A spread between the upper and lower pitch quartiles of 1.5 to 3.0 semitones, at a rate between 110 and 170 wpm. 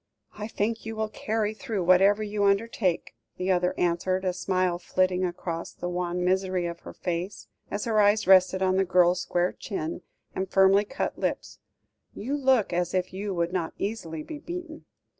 No: average, 2.7 semitones; average, 180 wpm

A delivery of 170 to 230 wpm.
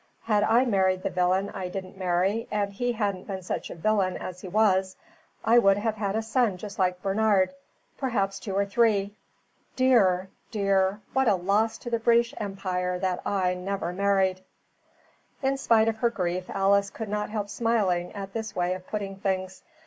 Yes: average, 180 wpm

